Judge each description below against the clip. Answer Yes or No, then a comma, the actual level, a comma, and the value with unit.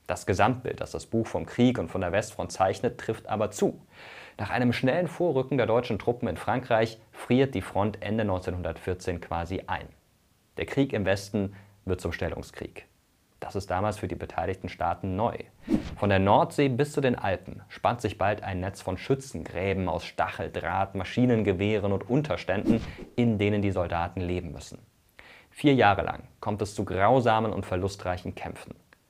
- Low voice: Yes, low, 100 Hz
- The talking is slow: No, average, 165 wpm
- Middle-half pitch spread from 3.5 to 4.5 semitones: Yes, average, 4.1 semitones